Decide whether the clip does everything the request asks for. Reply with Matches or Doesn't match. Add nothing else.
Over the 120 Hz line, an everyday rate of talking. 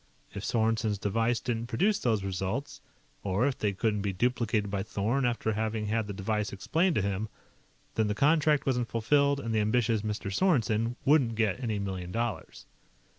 Doesn't match